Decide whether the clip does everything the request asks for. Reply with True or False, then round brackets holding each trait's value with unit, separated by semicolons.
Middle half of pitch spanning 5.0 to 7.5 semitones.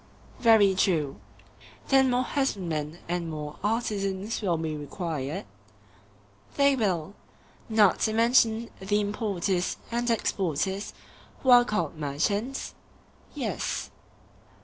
True (5.4 semitones)